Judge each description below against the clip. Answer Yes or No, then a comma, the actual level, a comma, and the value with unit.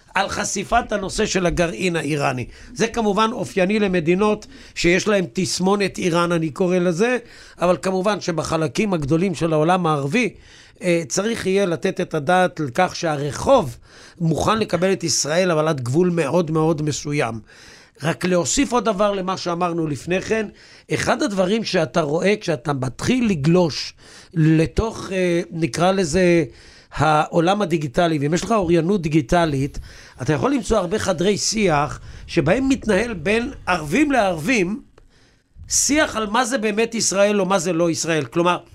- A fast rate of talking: No, average, 140 wpm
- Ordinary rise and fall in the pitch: Yes, average, 3.8 semitones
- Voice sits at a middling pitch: Yes, medium, 180 Hz